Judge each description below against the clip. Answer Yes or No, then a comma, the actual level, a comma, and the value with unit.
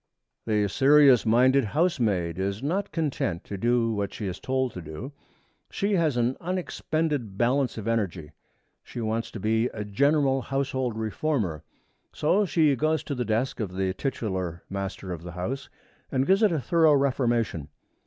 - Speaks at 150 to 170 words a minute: Yes, average, 165 wpm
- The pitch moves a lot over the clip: Yes, wide, 6.0 semitones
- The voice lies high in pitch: No, low, 120 Hz